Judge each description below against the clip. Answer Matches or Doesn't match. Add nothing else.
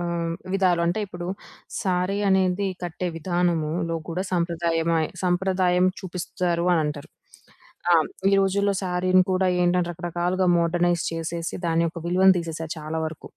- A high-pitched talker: Doesn't match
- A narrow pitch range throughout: Matches